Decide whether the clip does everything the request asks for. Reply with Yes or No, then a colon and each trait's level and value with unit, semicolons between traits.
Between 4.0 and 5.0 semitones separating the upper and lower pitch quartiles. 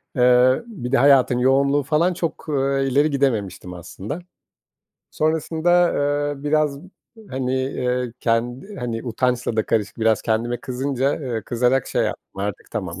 No: average, 3.2 semitones